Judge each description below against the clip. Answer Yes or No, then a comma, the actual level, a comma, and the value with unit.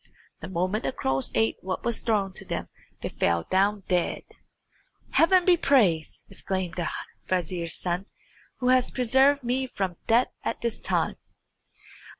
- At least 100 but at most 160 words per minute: Yes, average, 150 wpm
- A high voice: Yes, high, 195 Hz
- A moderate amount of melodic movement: No, wide, 6.0 semitones